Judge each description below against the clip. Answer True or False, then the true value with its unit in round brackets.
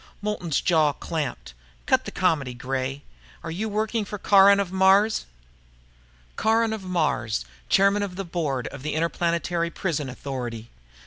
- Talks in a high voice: False (170 Hz)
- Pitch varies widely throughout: True (6.2 semitones)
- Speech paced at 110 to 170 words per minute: True (140 wpm)